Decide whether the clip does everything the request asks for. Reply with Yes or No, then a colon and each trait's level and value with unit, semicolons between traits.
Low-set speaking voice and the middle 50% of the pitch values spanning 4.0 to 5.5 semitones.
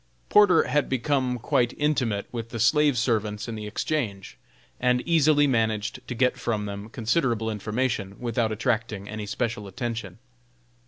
No: low, 115 Hz; average, 3.3 semitones